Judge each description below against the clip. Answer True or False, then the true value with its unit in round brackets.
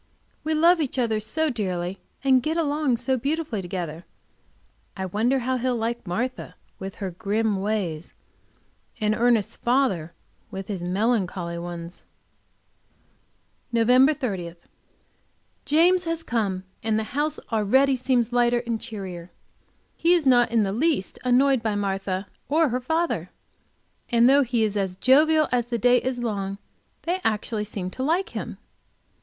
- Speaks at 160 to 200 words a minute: False (145 wpm)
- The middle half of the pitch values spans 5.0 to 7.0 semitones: True (5.3 semitones)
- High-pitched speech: True (235 Hz)